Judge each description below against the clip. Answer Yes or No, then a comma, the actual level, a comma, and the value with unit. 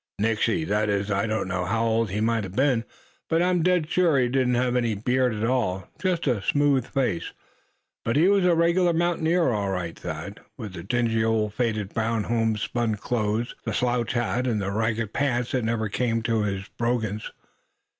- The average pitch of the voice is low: Yes, low, 115 Hz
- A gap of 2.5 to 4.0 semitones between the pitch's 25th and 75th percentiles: Yes, average, 3.5 semitones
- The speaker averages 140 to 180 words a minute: No, average, 190 wpm